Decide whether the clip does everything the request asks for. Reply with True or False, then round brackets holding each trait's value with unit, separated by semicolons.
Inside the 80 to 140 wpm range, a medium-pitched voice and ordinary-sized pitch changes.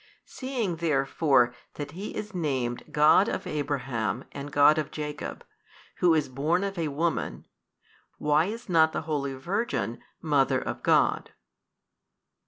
True (135 wpm; 150 Hz; 3.7 semitones)